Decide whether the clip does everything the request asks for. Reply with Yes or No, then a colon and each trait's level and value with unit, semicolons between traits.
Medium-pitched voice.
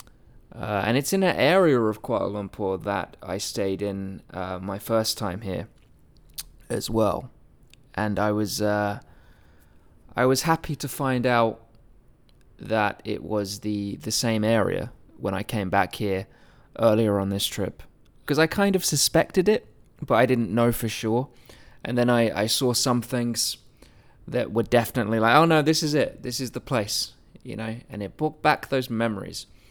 No: low, 115 Hz